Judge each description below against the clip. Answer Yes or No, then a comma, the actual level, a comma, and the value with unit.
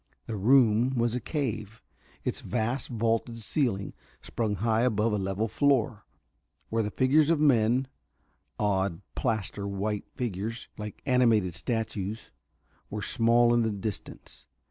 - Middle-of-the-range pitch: No, low, 110 Hz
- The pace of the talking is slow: Yes, slow, 130 wpm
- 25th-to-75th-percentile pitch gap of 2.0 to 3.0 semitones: Yes, narrow, 2.6 semitones